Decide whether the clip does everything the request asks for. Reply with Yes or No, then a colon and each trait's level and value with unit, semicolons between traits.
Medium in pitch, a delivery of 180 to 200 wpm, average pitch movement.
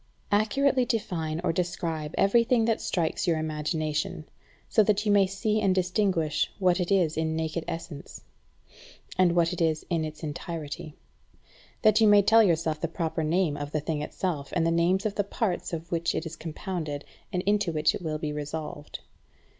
Yes: medium, 170 Hz; average, 185 wpm; average, 3.9 semitones